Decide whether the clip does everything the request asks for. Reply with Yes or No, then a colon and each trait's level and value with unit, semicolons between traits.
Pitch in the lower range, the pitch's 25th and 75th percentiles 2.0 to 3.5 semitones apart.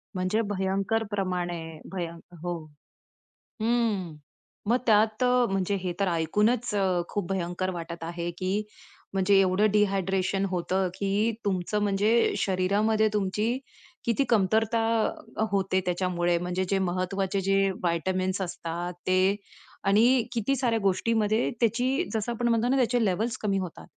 No: high, 195 Hz; average, 3.2 semitones